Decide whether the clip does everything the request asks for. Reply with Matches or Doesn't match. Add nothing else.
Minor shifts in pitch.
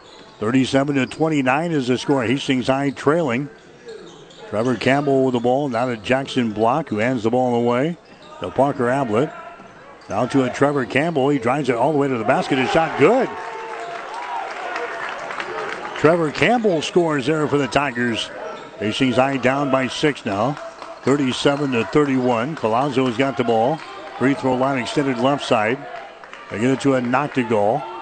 Matches